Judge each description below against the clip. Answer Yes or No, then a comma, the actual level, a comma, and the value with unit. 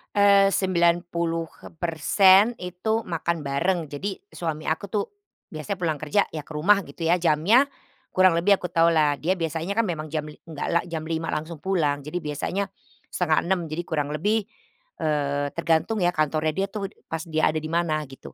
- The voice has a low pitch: No, medium, 165 Hz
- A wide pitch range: No, average, 3.3 semitones